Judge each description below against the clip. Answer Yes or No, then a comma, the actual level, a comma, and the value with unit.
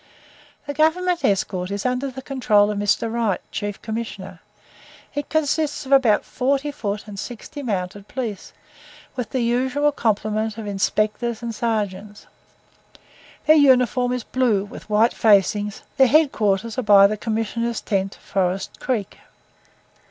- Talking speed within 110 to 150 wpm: Yes, average, 140 wpm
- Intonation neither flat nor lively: Yes, average, 4.1 semitones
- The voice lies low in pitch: No, high, 225 Hz